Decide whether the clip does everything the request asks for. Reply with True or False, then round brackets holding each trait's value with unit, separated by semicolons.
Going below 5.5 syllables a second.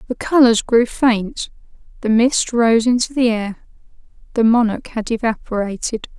True (4.4 syllables/s)